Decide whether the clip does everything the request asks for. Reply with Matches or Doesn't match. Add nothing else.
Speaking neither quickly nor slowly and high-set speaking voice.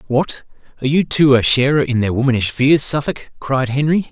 Doesn't match